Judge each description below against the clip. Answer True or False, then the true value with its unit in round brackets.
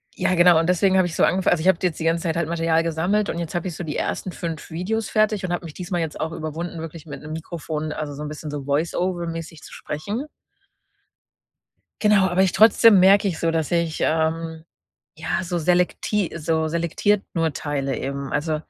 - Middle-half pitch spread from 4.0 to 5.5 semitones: False (2.4 semitones)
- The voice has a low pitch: False (165 Hz)